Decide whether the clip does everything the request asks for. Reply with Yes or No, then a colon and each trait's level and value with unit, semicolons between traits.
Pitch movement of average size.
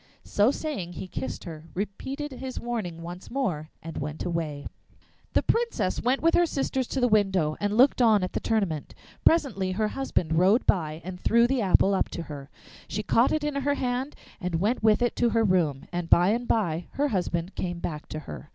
No: wide, 6.5 semitones